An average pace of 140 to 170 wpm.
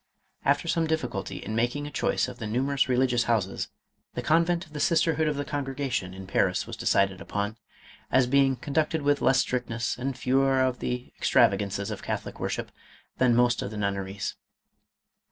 No: average, 190 wpm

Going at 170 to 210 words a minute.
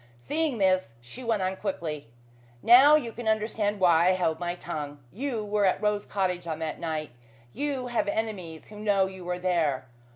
Yes: average, 185 wpm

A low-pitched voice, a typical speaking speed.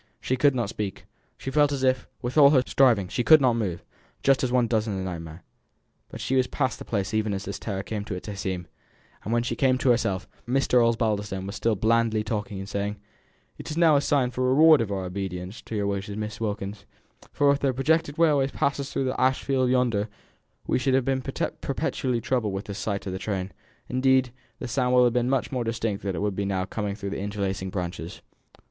No: low, 115 Hz; fast, 220 wpm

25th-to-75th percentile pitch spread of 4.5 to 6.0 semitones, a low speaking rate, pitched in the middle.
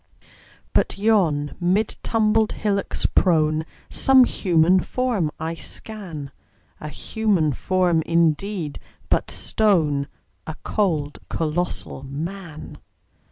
Yes: average, 5.0 semitones; slow, 95 wpm; medium, 175 Hz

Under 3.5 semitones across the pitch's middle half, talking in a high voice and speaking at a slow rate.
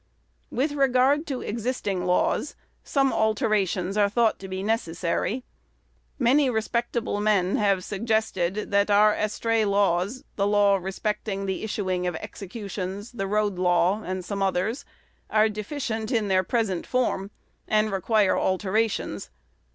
Yes: average, 2.9 semitones; high, 210 Hz; slow, 130 wpm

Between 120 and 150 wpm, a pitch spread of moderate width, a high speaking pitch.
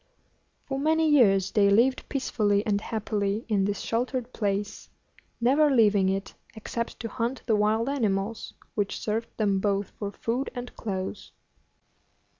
Yes: average, 140 wpm; average, 3.4 semitones; high, 215 Hz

